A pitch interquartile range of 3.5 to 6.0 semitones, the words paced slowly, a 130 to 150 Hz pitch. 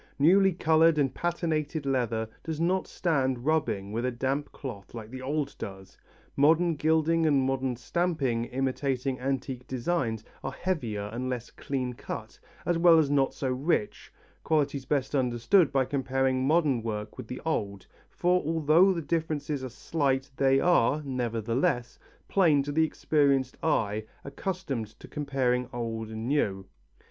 No: average, 4.2 semitones; average, 150 wpm; low, 135 Hz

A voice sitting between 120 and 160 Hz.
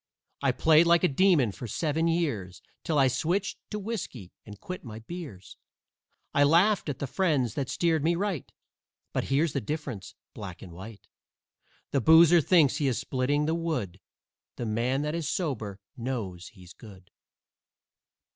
Yes: medium, 140 Hz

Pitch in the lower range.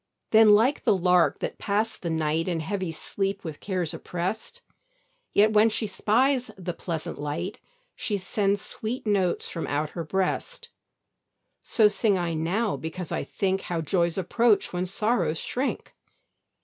No: high, 190 Hz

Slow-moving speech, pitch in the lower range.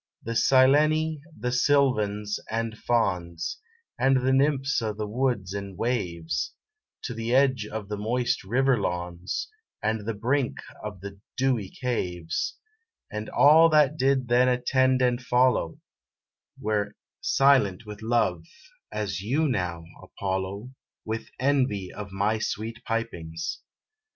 Yes: slow, 125 wpm; low, 115 Hz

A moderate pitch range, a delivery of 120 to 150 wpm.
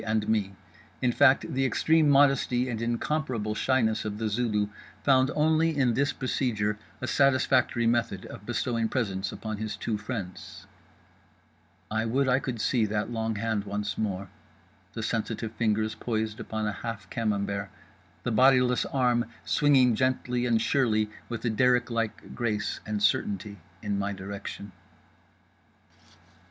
Yes: average, 3.3 semitones; average, 145 wpm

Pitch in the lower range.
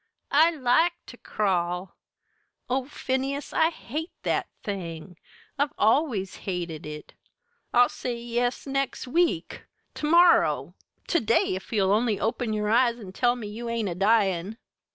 No: high, 230 Hz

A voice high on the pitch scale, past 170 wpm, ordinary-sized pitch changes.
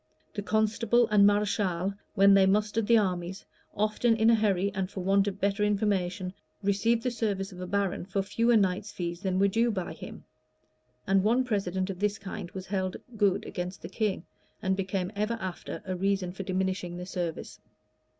No: high, 195 Hz; average, 185 wpm; narrow, 2.1 semitones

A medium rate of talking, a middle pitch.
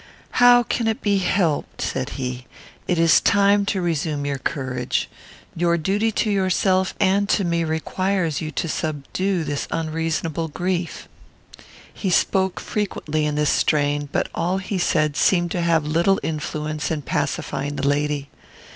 Yes: average, 150 wpm; medium, 165 Hz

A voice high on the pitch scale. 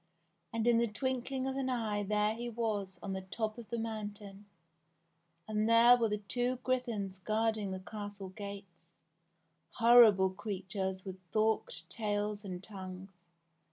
Yes: high, 210 Hz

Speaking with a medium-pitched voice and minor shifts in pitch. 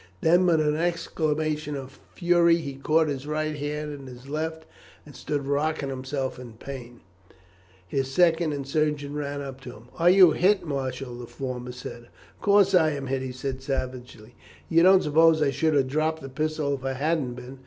No: medium, 145 Hz; average, 3.1 semitones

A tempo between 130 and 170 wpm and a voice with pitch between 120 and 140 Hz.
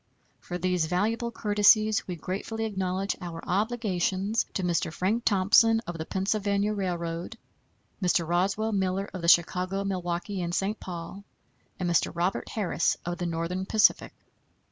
No: average, 145 wpm; high, 190 Hz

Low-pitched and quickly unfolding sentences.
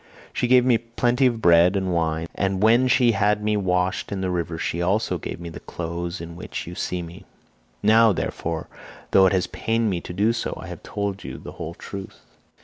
Yes: very low, 95 Hz; fast, 220 wpm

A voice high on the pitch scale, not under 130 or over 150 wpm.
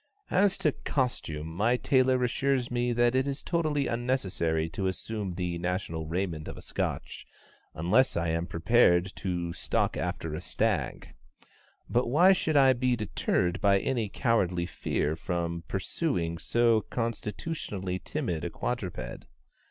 No: low, 105 Hz; average, 140 wpm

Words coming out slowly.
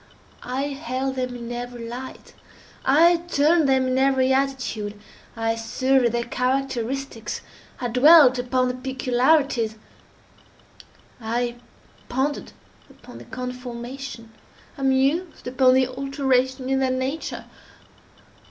Yes: slow, 110 wpm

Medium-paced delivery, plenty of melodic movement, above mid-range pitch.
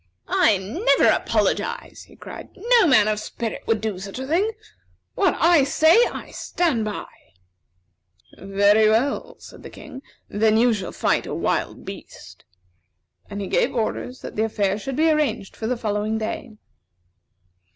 Yes: average, 155 wpm; wide, 6.5 semitones; high, 225 Hz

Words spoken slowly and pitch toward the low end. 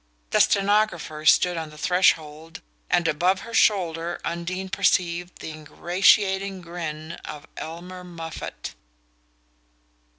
No: slow, 105 wpm; medium, 175 Hz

